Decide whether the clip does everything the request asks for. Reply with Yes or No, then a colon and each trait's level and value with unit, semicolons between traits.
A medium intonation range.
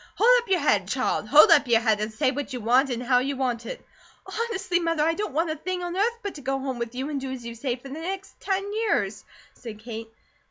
No: wide, 6.9 semitones